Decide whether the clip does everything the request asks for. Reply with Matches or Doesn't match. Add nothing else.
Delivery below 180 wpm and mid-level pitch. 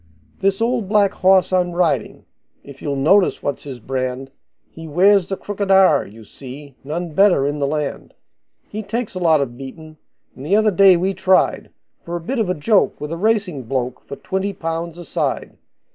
Doesn't match